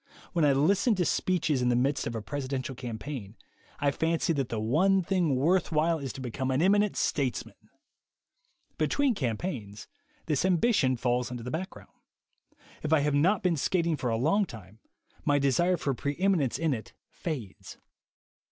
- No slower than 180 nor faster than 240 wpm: No, average, 170 wpm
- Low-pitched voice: No, medium, 145 Hz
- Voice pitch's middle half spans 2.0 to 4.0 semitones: No, wide, 5.5 semitones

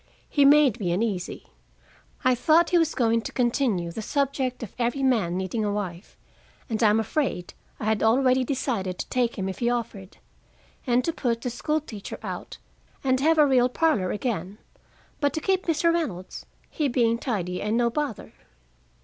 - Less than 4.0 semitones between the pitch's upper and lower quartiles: No, average, 5.0 semitones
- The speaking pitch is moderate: No, high, 240 Hz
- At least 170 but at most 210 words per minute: Yes, average, 175 wpm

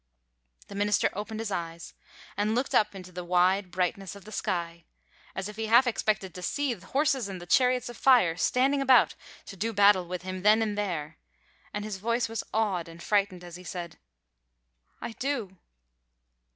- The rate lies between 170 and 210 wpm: Yes, average, 180 wpm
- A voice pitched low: No, high, 200 Hz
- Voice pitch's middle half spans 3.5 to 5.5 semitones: Yes, average, 3.8 semitones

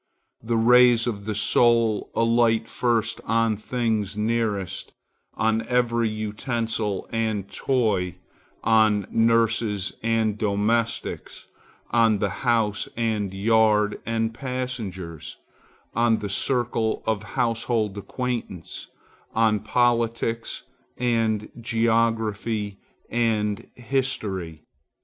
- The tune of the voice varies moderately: No, narrow, 1.8 semitones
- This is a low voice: Yes, low, 115 Hz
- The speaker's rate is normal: No, slow, 90 wpm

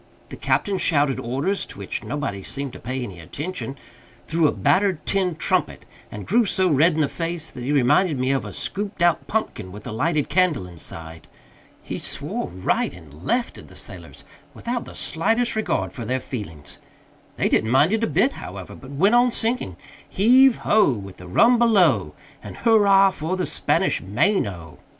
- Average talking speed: Yes, average, 185 wpm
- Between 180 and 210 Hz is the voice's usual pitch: No, medium, 155 Hz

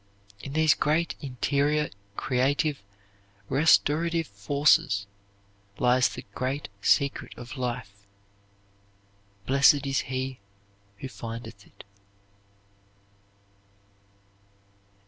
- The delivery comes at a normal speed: No, slow, 75 wpm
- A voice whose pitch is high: No, low, 135 Hz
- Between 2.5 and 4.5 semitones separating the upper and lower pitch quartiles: Yes, average, 3.2 semitones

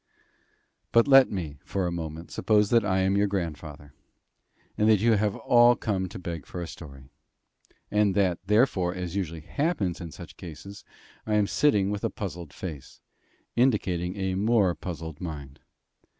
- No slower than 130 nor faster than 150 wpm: No, average, 165 wpm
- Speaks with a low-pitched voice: Yes, very low, 95 Hz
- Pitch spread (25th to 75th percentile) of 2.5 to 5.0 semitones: Yes, average, 3.9 semitones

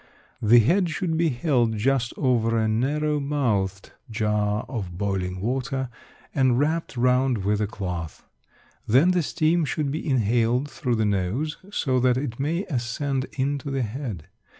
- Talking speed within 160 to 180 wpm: No, average, 150 wpm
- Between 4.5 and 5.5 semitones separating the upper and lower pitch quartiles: Yes, average, 4.9 semitones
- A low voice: Yes, low, 125 Hz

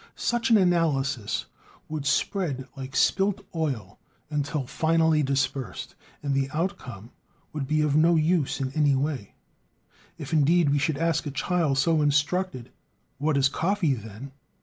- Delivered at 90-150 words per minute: Yes, average, 145 wpm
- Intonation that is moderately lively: Yes, average, 3.5 semitones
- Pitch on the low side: No, medium, 150 Hz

